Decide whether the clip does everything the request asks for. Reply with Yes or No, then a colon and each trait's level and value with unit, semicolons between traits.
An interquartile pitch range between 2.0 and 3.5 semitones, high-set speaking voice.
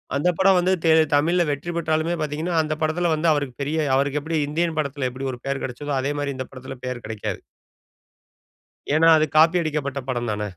No: average, 3.1 semitones; medium, 150 Hz